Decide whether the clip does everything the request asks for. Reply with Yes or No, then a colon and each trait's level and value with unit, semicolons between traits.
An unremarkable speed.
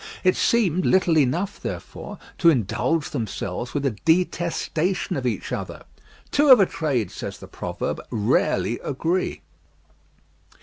No: slow, 130 wpm